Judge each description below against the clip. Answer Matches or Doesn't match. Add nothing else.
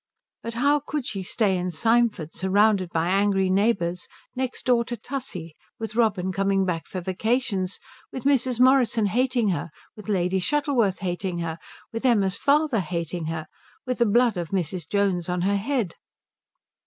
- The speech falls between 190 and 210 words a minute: Doesn't match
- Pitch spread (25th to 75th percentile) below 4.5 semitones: Doesn't match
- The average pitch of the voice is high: Matches